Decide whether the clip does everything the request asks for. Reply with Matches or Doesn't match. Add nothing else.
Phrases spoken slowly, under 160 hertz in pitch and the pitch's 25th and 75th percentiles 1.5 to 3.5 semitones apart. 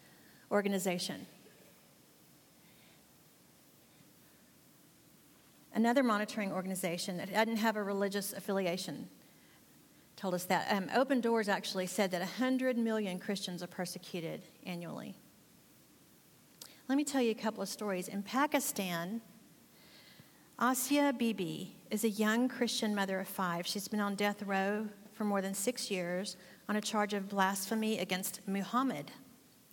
Doesn't match